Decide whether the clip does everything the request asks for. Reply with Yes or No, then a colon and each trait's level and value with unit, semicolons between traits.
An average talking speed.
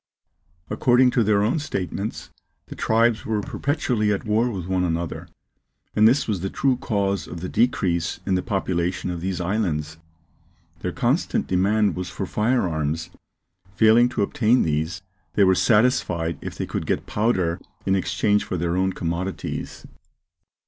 Yes: average, 155 wpm